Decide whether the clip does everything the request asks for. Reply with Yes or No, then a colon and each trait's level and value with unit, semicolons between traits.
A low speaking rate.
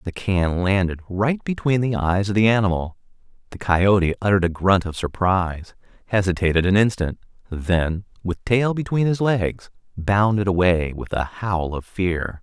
No: average, 160 wpm